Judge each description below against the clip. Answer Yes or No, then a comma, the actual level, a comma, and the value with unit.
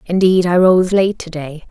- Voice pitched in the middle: Yes, medium, 175 Hz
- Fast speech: Yes, fast, 210 wpm